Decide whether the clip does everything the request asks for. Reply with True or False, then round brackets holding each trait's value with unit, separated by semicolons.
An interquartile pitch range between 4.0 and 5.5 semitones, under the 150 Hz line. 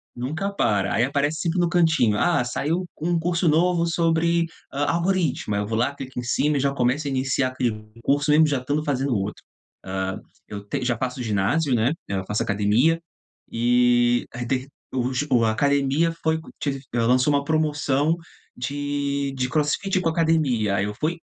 True (4.7 semitones; 140 Hz)